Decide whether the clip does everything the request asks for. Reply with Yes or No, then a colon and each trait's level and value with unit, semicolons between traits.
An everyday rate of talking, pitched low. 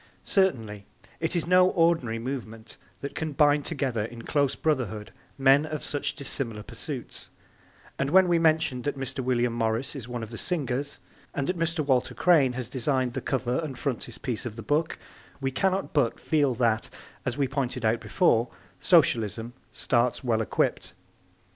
Yes: average, 165 wpm; low, 130 Hz